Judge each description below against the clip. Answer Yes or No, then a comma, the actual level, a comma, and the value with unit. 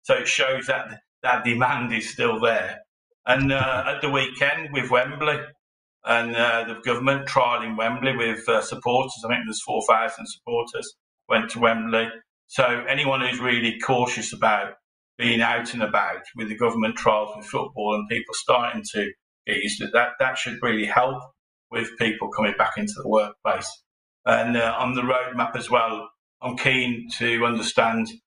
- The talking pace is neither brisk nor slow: Yes, average, 170 wpm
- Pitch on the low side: Yes, low, 120 Hz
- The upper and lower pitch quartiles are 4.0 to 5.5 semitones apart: No, narrow, 2.5 semitones